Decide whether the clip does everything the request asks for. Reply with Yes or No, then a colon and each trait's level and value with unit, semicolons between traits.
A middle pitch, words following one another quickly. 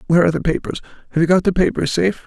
Yes: medium, 170 Hz; fast, 240 wpm